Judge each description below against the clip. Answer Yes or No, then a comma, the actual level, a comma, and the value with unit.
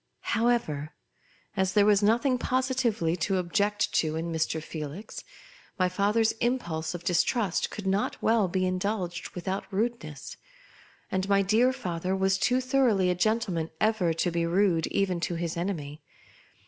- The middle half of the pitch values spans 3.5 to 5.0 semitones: Yes, average, 4.2 semitones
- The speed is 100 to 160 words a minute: Yes, average, 150 wpm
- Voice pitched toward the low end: No, high, 190 Hz